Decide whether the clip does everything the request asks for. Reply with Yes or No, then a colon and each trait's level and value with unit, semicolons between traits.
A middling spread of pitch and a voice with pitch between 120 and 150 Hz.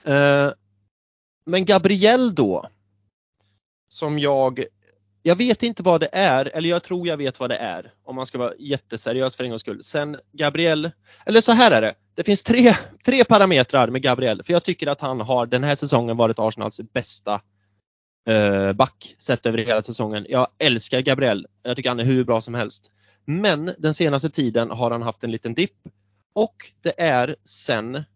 No: wide, 6.5 semitones; low, 130 Hz